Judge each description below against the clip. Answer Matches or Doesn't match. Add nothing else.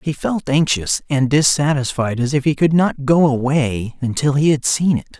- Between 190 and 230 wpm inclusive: Matches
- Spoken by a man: Matches